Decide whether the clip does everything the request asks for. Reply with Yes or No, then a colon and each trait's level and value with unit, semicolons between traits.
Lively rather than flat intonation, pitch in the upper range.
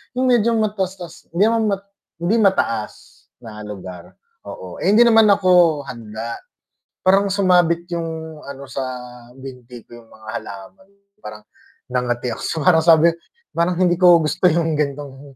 No: wide, 7.1 semitones; medium, 165 Hz